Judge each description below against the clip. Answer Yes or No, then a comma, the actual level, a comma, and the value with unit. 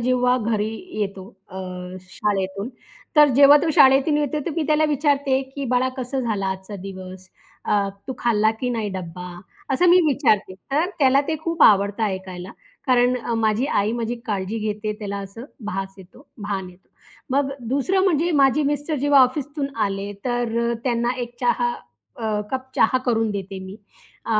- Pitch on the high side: Yes, high, 235 Hz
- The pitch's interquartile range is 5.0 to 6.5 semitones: Yes, wide, 5.4 semitones